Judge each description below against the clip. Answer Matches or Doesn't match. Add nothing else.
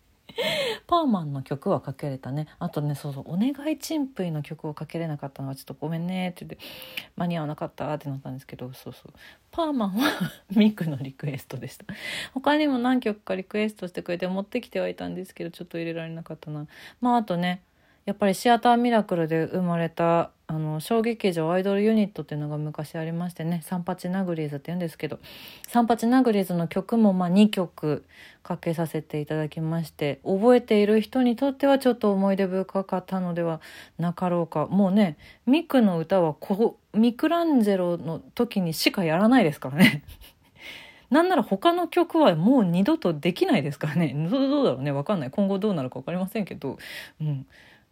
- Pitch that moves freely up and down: Matches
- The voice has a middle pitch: Matches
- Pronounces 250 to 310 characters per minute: Doesn't match